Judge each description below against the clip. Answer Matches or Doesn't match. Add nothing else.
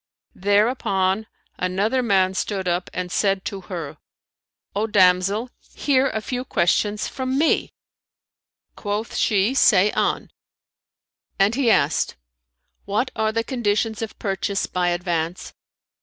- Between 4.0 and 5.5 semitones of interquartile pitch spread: Doesn't match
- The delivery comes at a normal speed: Doesn't match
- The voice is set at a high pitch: Matches